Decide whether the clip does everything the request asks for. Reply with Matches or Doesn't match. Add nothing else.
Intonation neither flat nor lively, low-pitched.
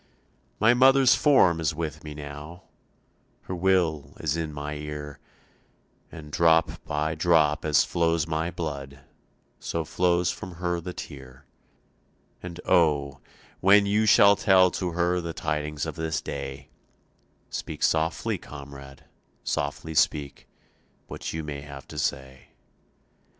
Matches